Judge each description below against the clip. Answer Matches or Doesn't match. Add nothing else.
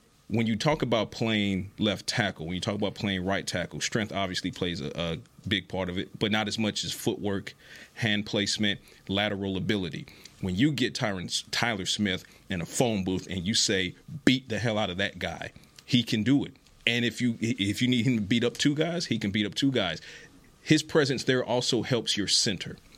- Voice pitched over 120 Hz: Doesn't match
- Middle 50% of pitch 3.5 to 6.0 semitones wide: Matches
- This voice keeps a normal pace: Doesn't match